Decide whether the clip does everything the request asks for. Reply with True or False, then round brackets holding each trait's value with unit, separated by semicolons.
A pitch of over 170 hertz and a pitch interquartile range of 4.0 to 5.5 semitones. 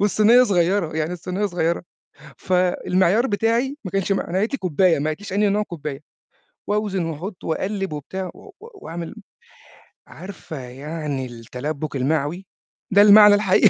True (185 Hz; 4.7 semitones)